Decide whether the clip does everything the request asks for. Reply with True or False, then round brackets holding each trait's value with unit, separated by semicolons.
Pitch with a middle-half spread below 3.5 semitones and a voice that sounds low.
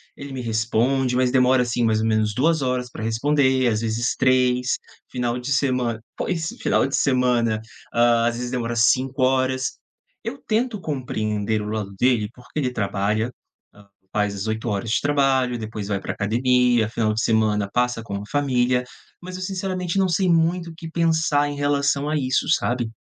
False (3.9 semitones; 125 Hz)